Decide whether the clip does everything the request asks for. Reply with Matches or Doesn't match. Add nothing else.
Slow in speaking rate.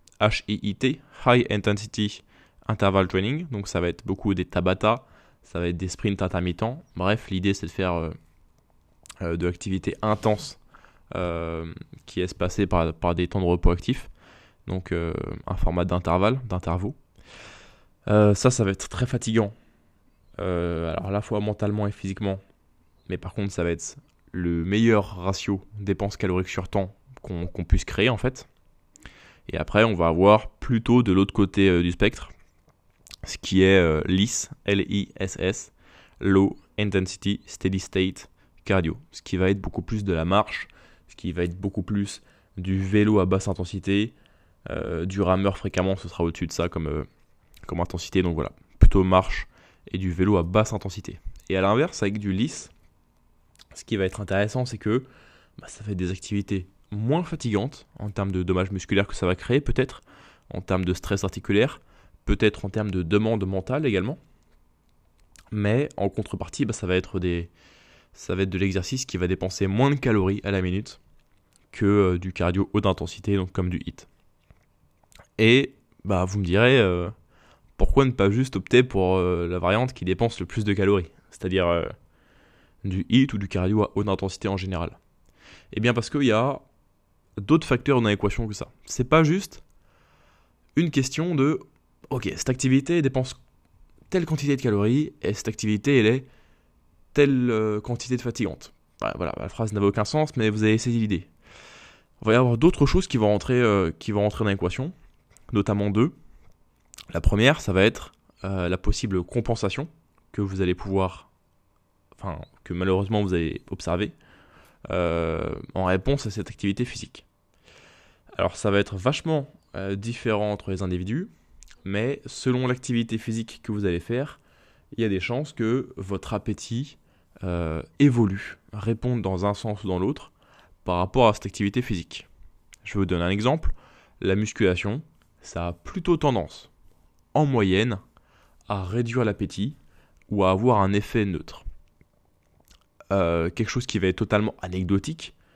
Doesn't match